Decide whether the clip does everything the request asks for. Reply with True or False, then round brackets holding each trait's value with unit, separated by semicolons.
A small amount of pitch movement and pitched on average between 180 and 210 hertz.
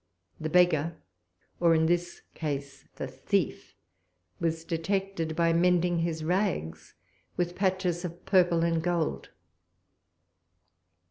False (1.7 semitones; 170 Hz)